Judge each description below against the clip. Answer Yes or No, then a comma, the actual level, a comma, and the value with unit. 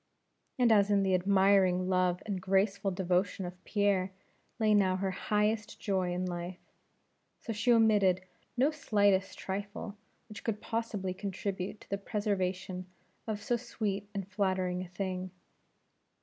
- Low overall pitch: No, high, 195 Hz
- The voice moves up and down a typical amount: No, narrow, 2.1 semitones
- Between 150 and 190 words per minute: No, average, 140 wpm